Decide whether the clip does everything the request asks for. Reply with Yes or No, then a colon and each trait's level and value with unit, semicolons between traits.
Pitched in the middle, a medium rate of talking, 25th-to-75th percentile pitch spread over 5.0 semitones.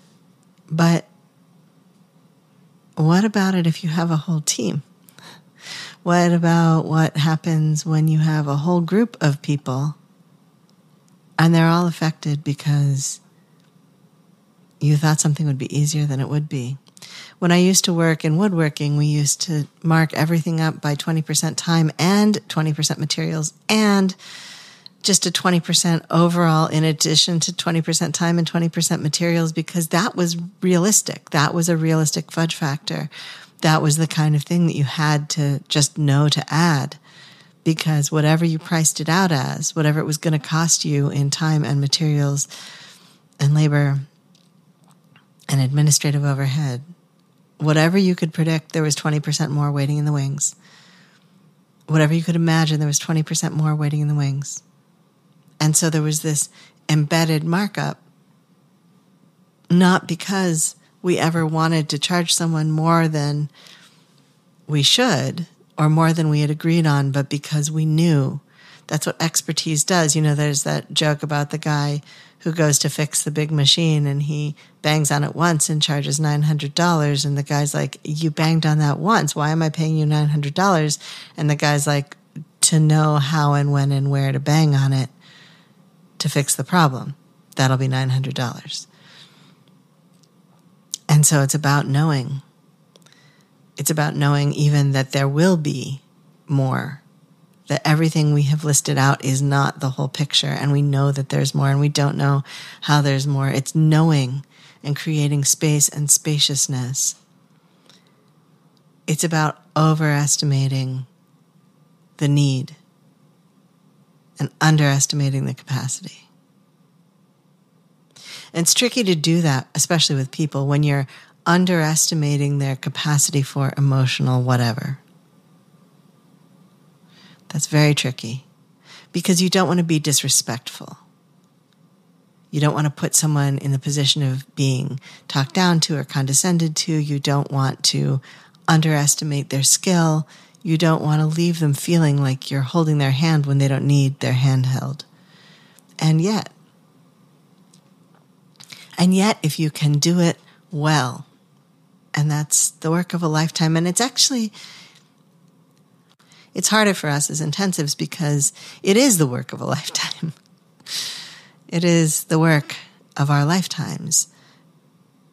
No: medium, 160 Hz; average, 145 wpm; average, 2.8 semitones